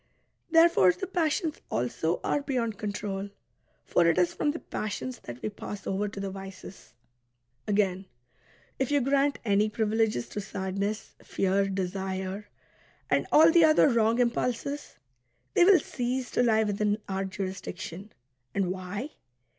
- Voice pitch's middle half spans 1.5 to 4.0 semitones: No, average, 4.7 semitones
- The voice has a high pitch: Yes, high, 205 Hz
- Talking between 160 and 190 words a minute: No, average, 140 wpm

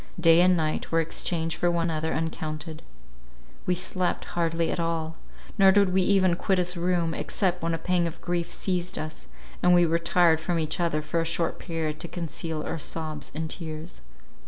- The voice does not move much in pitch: Yes, narrow, 1.7 semitones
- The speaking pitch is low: No, medium, 165 Hz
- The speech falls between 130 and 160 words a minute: No, average, 185 wpm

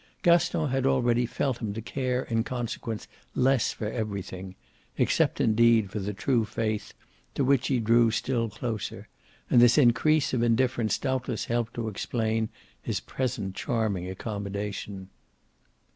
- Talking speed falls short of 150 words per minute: Yes, average, 140 wpm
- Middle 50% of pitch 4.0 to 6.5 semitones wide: No, average, 3.0 semitones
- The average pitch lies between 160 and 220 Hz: No, low, 115 Hz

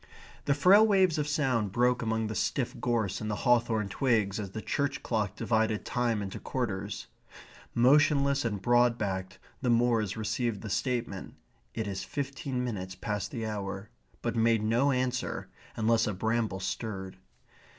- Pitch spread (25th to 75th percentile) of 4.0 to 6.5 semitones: No, average, 3.2 semitones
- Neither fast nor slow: Yes, average, 155 wpm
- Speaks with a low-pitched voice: Yes, low, 115 Hz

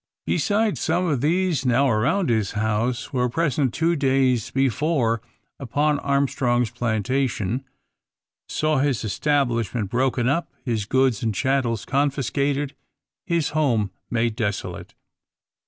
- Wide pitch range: No, average, 3.8 semitones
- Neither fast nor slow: No, slow, 115 wpm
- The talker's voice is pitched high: No, low, 130 Hz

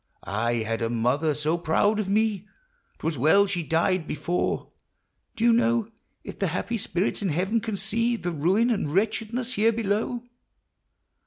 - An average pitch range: No, wide, 5.8 semitones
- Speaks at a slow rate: No, average, 170 wpm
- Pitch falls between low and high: No, high, 195 Hz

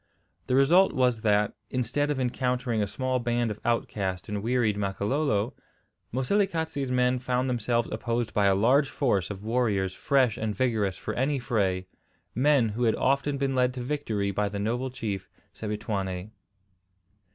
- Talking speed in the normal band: Yes, average, 155 wpm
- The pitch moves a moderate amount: Yes, average, 4.0 semitones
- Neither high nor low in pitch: No, low, 120 Hz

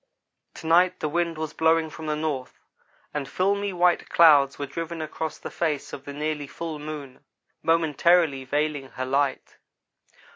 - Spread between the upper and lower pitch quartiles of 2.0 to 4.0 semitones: Yes, average, 2.7 semitones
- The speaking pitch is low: No, medium, 155 Hz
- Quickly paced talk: No, average, 155 wpm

